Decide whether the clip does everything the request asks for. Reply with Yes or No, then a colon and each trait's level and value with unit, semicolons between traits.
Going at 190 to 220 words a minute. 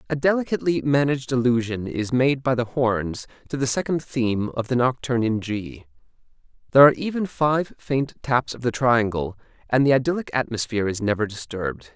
No: average, 170 wpm